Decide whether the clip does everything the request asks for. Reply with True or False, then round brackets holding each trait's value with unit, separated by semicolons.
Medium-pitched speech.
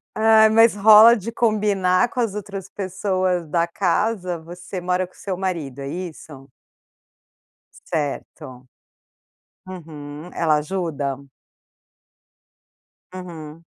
True (180 Hz)